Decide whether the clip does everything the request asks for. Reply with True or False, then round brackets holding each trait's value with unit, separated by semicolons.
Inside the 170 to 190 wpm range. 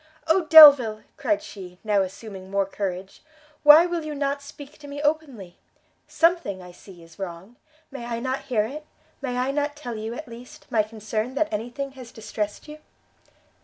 True (180 wpm)